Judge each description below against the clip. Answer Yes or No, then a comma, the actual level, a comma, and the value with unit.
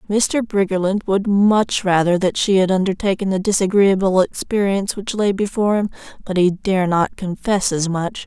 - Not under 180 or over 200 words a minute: No, average, 165 wpm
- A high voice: Yes, high, 195 Hz